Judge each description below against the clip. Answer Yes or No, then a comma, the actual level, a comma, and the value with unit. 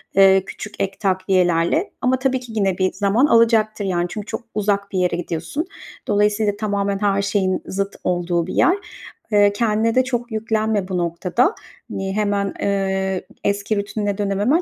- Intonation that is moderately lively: No, narrow, 2.1 semitones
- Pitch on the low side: No, high, 200 Hz